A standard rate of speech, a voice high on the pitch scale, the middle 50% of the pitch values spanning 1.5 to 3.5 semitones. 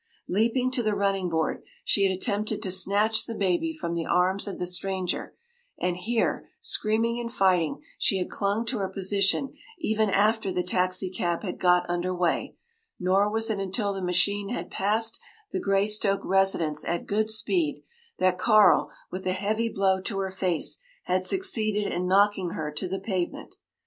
Yes: average, 170 wpm; high, 195 Hz; average, 2.8 semitones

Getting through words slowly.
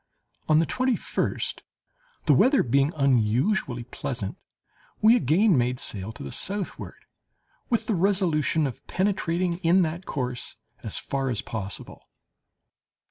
Yes: slow, 130 wpm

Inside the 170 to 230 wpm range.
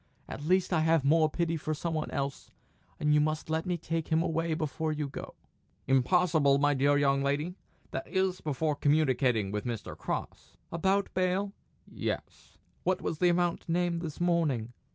Yes: average, 175 wpm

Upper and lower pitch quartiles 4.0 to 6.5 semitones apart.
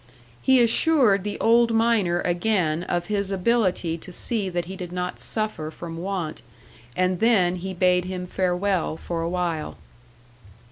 No: average, 3.1 semitones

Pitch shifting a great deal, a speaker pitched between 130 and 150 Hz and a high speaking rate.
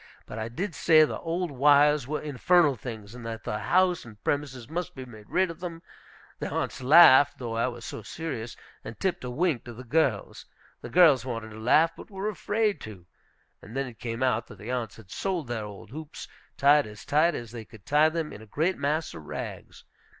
Yes: wide, 6.1 semitones; low, 135 Hz; fast, 215 wpm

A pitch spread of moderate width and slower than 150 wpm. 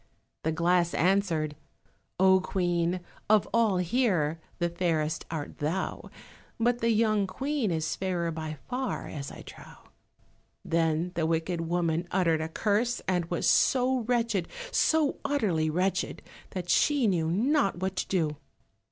Yes: average, 4.7 semitones; average, 140 wpm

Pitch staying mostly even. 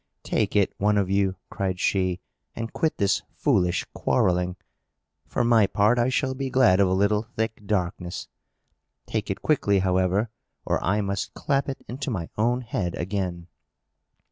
No: average, 4.0 semitones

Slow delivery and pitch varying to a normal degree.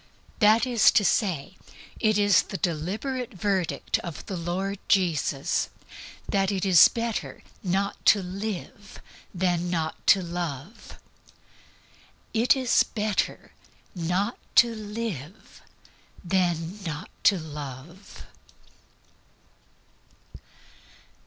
Yes: slow, 95 wpm; average, 3.5 semitones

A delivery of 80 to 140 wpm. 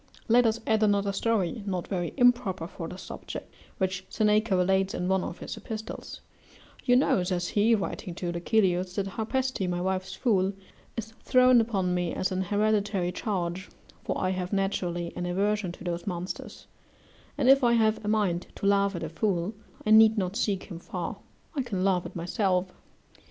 No: average, 180 wpm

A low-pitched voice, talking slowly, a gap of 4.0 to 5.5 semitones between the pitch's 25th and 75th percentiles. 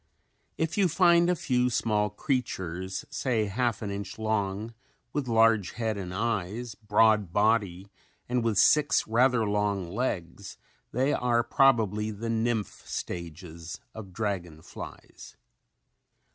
No: low, 110 Hz; slow, 125 wpm; average, 3.5 semitones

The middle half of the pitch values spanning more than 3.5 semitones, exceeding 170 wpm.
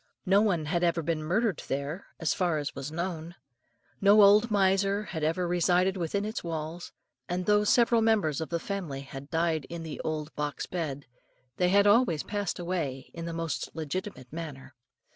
Yes: average, 4.1 semitones; average, 180 wpm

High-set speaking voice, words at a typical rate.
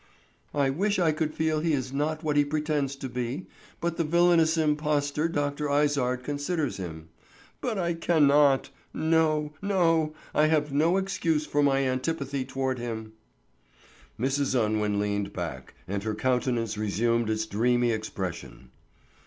No: medium, 145 Hz; average, 145 wpm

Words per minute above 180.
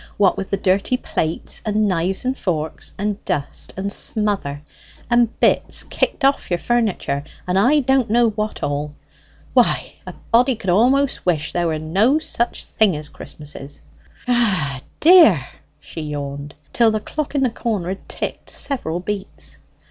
No: average, 160 wpm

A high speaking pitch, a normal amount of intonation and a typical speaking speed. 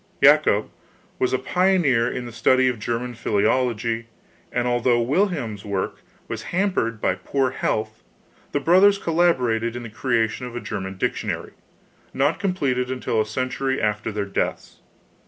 No: low, 125 Hz; average, 3.6 semitones; average, 145 wpm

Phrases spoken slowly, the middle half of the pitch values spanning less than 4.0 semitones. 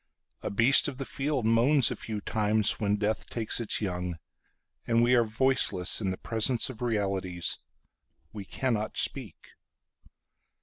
Yes: slow, 130 wpm; average, 3.3 semitones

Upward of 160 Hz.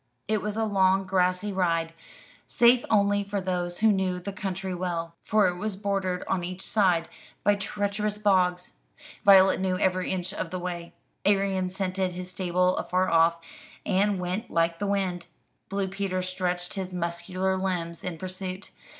Yes: medium, 185 Hz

